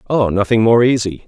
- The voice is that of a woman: No, male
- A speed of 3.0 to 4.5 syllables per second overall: No, 5.6 syllables/s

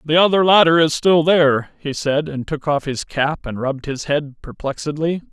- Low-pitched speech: No, medium, 150 Hz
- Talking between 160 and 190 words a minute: No, fast, 205 wpm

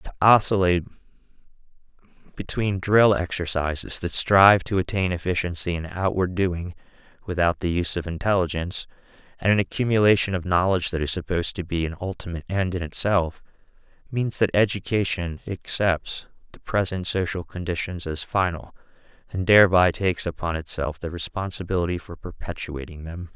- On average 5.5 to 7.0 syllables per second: Yes, 5.6 syllables/s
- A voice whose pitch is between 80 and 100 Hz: Yes, very low, 90 Hz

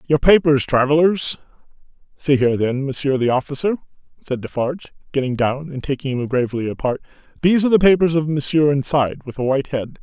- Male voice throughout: Yes, male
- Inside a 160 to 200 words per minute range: Yes, average, 175 wpm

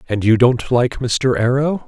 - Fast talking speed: No, average, 190 wpm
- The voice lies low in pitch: Yes, low, 125 Hz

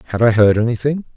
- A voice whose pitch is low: Yes, low, 120 Hz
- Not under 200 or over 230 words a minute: Yes, fast, 205 wpm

